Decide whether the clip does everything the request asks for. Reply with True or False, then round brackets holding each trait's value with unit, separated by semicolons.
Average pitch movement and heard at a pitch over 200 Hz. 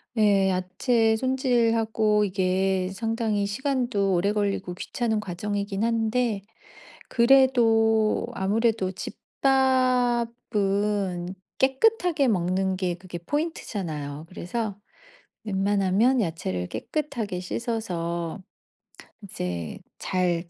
True (4.2 semitones; 210 Hz)